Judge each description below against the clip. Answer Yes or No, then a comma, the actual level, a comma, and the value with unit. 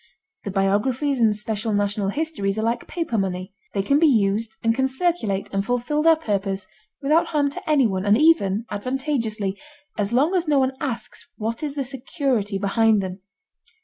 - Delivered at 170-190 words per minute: Yes, average, 175 wpm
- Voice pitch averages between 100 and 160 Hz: No, high, 230 Hz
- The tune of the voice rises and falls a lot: Yes, wide, 5.8 semitones